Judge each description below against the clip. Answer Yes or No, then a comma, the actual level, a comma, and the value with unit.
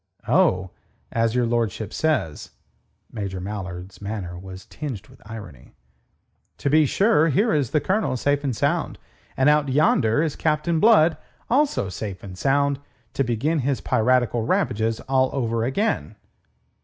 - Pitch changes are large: Yes, wide, 6.2 semitones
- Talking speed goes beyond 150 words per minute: No, average, 145 wpm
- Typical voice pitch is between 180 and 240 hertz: No, low, 125 Hz